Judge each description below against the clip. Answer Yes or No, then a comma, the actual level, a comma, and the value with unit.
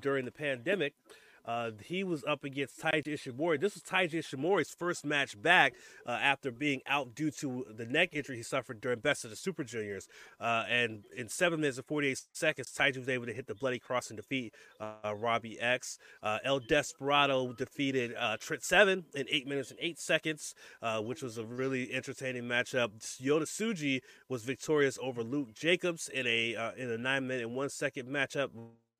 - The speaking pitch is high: No, low, 135 Hz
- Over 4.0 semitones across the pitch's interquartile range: No, average, 3.5 semitones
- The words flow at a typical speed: Yes, average, 190 wpm